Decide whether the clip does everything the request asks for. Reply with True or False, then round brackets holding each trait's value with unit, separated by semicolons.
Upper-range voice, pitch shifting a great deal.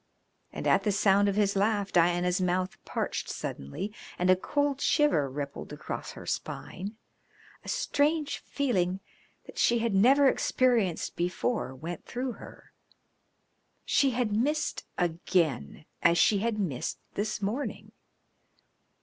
True (200 Hz; 5.7 semitones)